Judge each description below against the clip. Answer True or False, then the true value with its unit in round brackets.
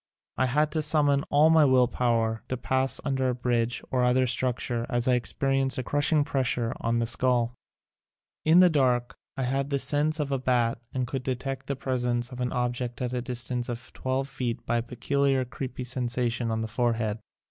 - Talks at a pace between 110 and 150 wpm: False (200 wpm)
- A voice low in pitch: True (125 Hz)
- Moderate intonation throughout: False (2.0 semitones)